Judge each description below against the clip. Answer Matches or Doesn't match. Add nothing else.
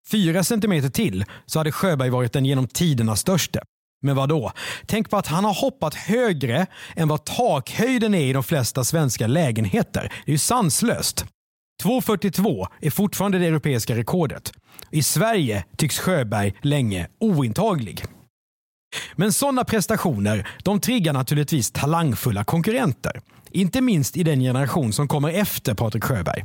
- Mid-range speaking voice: Matches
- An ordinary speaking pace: Matches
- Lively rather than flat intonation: Matches